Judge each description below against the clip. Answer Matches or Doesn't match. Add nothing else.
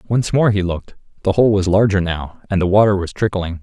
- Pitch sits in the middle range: Doesn't match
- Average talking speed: Doesn't match